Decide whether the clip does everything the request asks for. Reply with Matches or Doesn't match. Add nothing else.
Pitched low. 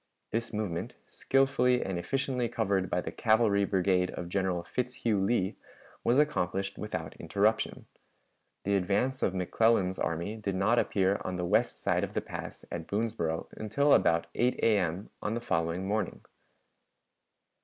Matches